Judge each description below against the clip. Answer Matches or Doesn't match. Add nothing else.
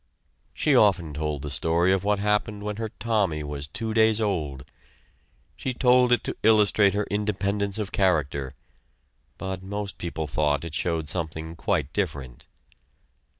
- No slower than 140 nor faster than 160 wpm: Matches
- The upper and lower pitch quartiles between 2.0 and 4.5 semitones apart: Doesn't match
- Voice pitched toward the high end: Doesn't match